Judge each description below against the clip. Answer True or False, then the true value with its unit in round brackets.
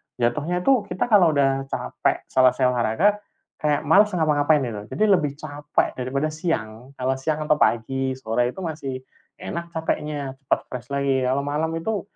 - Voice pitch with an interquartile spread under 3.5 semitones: False (3.8 semitones)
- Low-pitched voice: False (145 Hz)